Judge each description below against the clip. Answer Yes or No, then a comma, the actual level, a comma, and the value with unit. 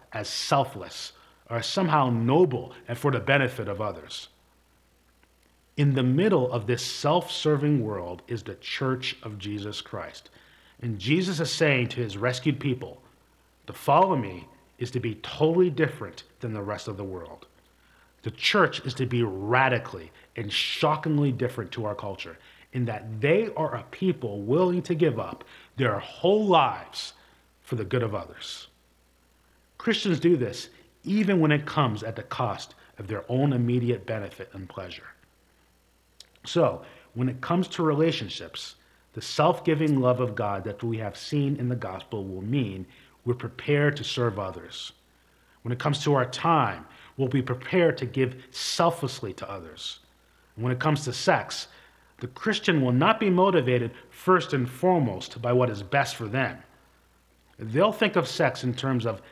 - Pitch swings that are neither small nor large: No, wide, 6.4 semitones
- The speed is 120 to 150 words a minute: No, average, 165 wpm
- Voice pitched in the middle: No, low, 125 Hz